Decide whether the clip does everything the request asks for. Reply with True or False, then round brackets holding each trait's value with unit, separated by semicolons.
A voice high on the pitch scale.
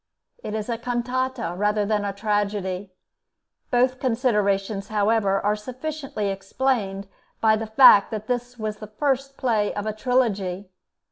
True (215 Hz)